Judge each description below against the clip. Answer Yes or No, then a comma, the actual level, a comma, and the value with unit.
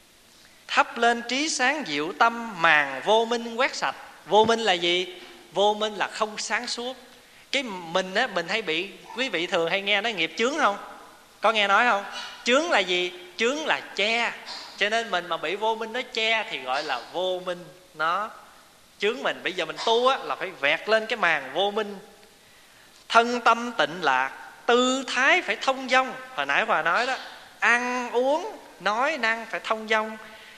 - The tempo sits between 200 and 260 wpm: No, average, 190 wpm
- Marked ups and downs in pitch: No, average, 4.2 semitones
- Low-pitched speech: No, high, 220 Hz